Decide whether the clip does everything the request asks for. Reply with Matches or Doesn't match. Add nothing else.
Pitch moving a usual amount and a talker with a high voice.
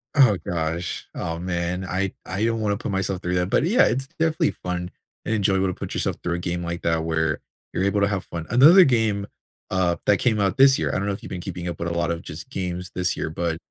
Doesn't match